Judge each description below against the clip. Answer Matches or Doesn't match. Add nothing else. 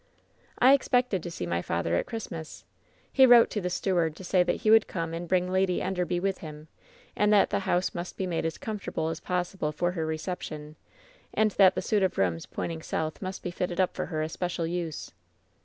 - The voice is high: Doesn't match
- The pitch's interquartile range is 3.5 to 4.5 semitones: Doesn't match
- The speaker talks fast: Matches